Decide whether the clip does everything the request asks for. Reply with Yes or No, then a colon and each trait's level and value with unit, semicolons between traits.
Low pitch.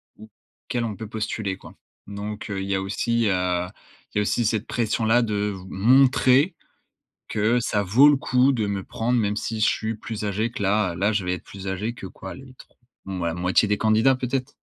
Yes: low, 110 Hz